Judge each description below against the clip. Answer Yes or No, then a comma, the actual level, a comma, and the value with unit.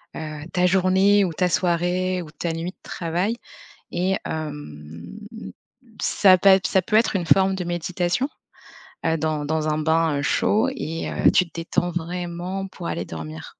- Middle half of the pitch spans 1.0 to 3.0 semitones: Yes, average, 2.7 semitones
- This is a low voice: No, medium, 175 Hz